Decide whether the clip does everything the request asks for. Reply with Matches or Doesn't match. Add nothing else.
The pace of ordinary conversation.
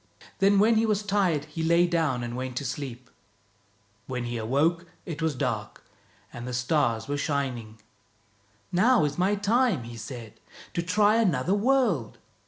Matches